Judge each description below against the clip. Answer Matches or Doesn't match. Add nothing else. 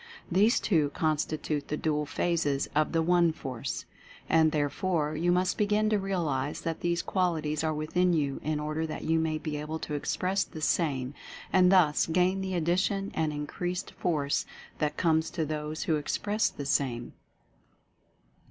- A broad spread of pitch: Doesn't match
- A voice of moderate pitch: Matches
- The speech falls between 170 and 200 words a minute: Doesn't match